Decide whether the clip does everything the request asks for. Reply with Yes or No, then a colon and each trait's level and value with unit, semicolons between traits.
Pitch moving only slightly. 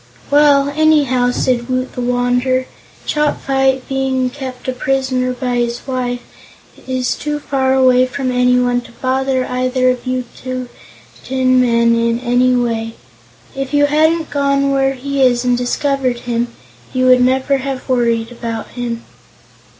Yes: narrow, 1.5 semitones